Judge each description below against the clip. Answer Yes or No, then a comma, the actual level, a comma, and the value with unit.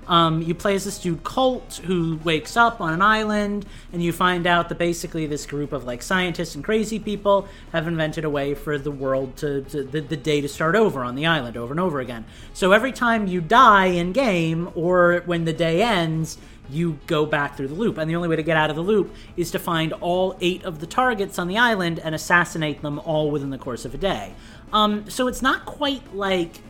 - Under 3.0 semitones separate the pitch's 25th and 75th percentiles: No, average, 4.4 semitones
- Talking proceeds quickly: Yes, fast, 235 wpm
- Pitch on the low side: No, medium, 170 Hz